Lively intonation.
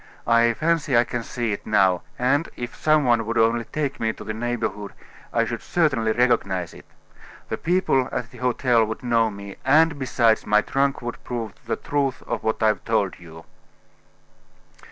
No: average, 3.2 semitones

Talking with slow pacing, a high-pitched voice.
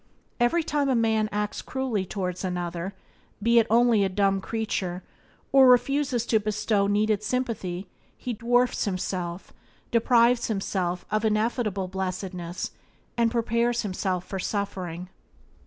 Yes: slow, 125 wpm; high, 210 Hz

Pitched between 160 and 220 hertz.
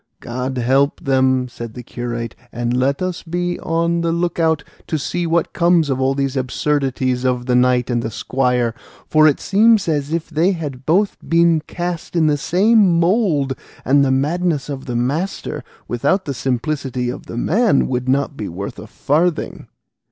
No: medium, 140 Hz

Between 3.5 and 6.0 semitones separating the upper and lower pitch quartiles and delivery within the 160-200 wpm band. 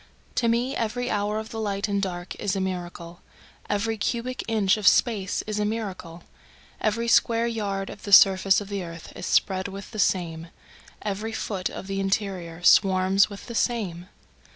No: average, 2.7 semitones; average, 175 wpm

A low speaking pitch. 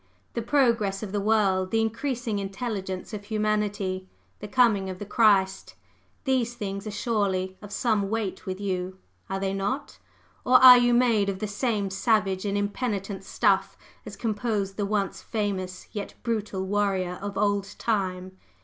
No: high, 205 Hz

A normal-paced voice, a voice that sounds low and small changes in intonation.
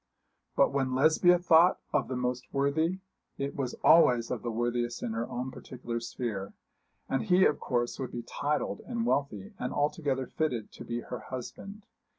No: average, 170 wpm; low, 130 Hz; average, 4.5 semitones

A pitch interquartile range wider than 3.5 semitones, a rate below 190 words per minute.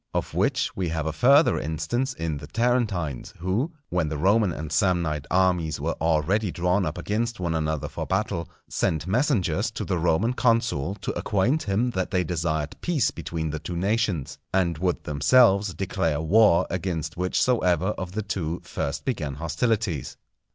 Yes: average, 5.1 semitones; average, 165 wpm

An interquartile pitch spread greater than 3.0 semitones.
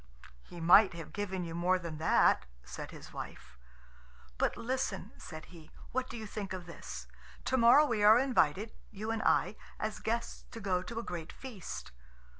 Yes: average, 4.9 semitones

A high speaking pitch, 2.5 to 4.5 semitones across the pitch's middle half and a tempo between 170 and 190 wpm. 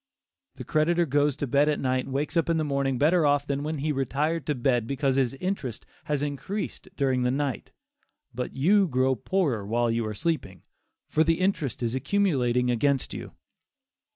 No: medium, 140 Hz; average, 3.5 semitones; average, 185 wpm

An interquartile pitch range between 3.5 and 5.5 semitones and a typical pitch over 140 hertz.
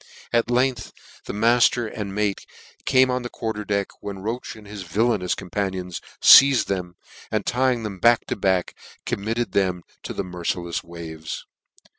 No: average, 4.3 semitones; low, 105 Hz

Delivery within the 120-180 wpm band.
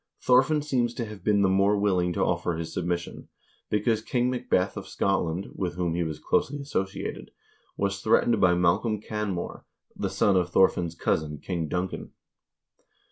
Yes: average, 160 wpm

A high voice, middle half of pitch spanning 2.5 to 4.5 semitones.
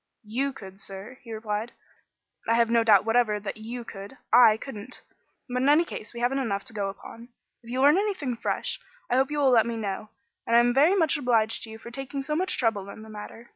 Yes: high, 235 Hz; average, 3.5 semitones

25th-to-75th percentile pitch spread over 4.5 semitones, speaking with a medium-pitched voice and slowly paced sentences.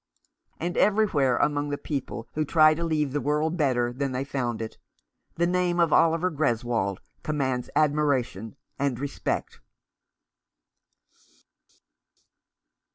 No: average, 3.8 semitones; medium, 145 Hz; slow, 115 wpm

